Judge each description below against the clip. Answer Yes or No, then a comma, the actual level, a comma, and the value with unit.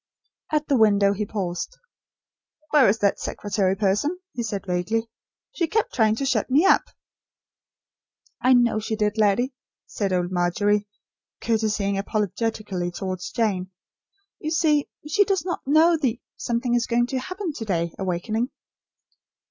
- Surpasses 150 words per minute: No, average, 145 wpm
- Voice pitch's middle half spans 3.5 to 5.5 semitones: Yes, average, 5.2 semitones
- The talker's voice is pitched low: No, high, 220 Hz